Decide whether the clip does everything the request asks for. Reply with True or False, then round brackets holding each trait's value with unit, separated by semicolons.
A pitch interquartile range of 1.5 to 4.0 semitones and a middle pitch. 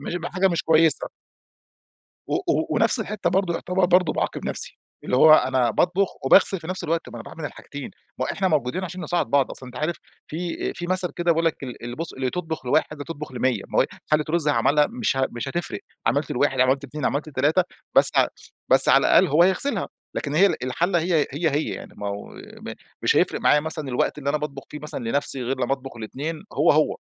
False (4.5 semitones; 155 Hz)